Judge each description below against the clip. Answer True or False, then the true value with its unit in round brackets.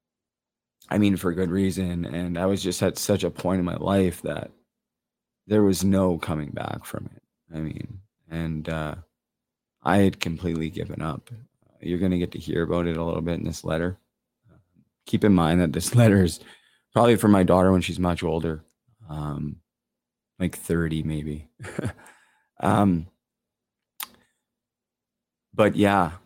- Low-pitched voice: True (90 Hz)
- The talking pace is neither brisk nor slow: True (160 wpm)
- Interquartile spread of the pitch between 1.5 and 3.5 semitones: True (2.8 semitones)